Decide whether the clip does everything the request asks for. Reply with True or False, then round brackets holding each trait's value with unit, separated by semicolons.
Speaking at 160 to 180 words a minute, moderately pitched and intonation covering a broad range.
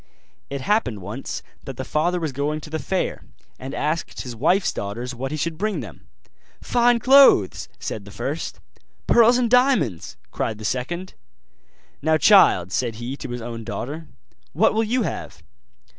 True (165 wpm; 150 Hz; 8.6 semitones)